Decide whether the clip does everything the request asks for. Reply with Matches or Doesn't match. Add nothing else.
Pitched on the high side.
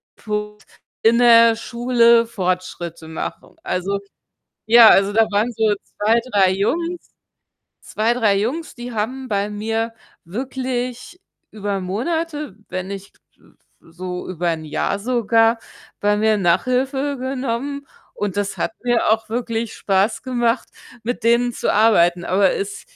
Matches